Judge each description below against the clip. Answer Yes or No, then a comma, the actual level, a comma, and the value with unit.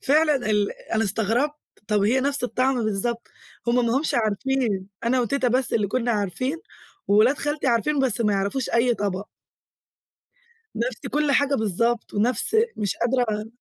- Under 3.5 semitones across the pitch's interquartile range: No, average, 3.9 semitones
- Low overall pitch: No, high, 235 Hz